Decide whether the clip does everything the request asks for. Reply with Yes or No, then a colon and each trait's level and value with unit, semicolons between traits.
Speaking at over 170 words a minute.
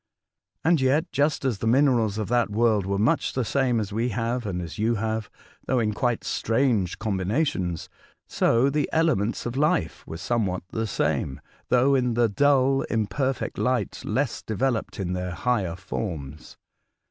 No: average, 165 wpm